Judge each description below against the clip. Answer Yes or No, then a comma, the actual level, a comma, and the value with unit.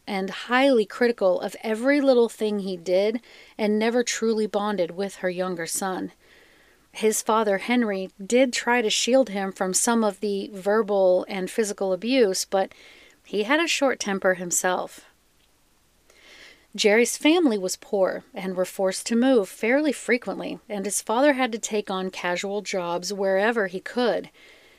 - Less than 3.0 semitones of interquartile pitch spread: No, average, 3.8 semitones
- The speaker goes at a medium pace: Yes, average, 155 wpm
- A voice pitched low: No, high, 210 Hz